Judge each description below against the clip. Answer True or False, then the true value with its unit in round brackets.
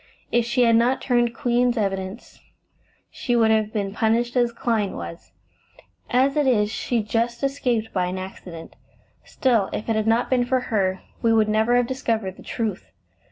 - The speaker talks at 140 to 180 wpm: True (175 wpm)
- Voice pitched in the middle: False (230 Hz)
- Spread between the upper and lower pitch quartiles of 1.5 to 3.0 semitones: True (2.6 semitones)